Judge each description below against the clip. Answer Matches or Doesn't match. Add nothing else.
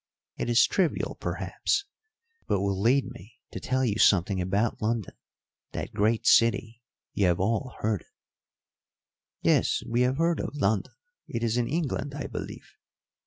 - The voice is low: Matches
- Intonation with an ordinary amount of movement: Matches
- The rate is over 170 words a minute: Doesn't match